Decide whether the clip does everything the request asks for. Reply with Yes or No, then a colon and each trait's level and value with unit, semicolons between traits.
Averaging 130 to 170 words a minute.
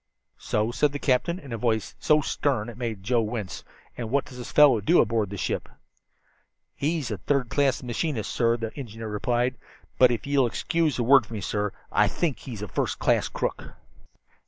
No: average, 195 wpm